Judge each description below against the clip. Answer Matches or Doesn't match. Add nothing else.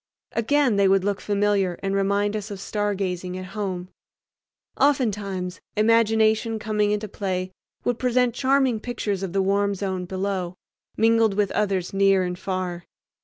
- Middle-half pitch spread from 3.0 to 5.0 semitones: Doesn't match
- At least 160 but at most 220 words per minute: Doesn't match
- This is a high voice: Matches